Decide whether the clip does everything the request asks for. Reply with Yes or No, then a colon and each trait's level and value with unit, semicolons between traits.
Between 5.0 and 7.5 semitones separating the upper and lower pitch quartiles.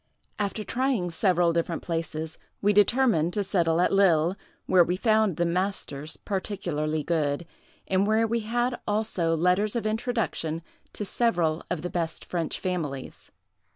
No: average, 4.5 semitones